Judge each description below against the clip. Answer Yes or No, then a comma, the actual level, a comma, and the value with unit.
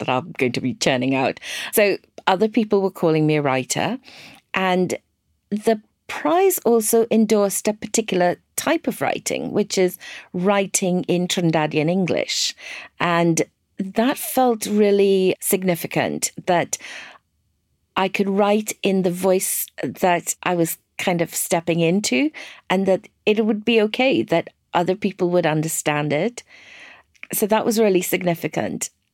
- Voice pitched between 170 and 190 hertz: Yes, medium, 185 Hz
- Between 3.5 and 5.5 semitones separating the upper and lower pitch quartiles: Yes, average, 4.5 semitones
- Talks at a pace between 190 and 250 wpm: No, average, 140 wpm